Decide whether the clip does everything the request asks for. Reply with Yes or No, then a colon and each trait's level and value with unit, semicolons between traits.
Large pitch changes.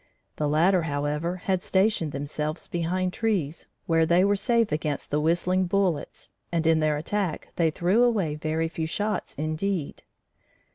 No: average, 3.6 semitones